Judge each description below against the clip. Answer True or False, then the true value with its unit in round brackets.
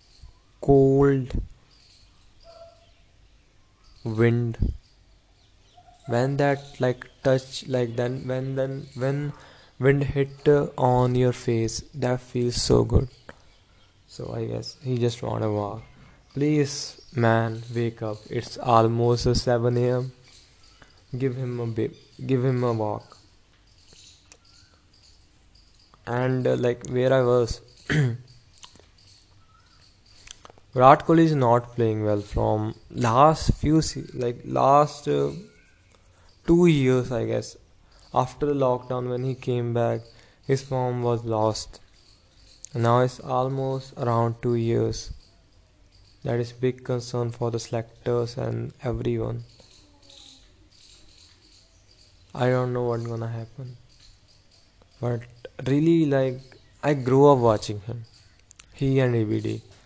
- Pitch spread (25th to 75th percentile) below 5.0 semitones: True (4.0 semitones)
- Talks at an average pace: False (110 wpm)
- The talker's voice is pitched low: True (115 Hz)